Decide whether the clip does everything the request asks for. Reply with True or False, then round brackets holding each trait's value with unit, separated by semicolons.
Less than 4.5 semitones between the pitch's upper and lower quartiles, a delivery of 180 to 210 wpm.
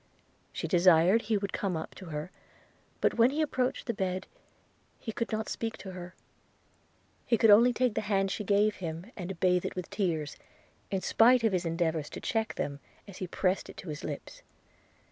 True (4.1 semitones; 200 wpm)